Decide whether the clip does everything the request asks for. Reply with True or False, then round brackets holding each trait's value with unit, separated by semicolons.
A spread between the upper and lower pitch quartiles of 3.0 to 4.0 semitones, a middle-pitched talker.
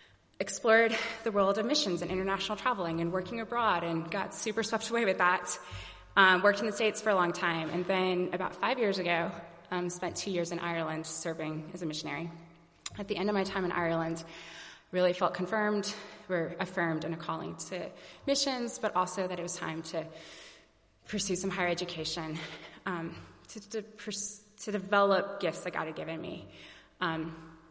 True (3.6 semitones; 180 Hz)